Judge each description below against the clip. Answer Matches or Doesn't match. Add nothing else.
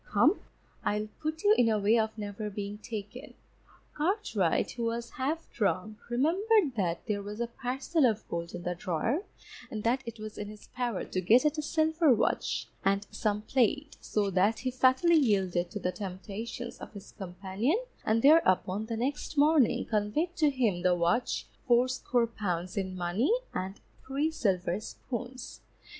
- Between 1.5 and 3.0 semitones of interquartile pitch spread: Doesn't match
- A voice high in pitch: Matches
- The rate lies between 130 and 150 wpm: Doesn't match